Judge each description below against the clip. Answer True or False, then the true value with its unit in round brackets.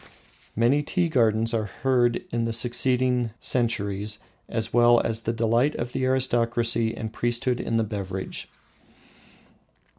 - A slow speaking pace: True (130 wpm)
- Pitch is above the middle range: False (115 Hz)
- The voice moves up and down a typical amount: False (1.7 semitones)